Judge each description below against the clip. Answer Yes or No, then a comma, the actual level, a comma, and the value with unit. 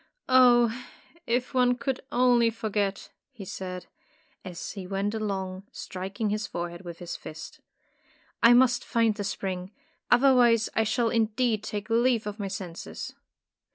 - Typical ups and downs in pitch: Yes, average, 3.9 semitones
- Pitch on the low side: No, high, 215 Hz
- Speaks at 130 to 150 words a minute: Yes, average, 145 wpm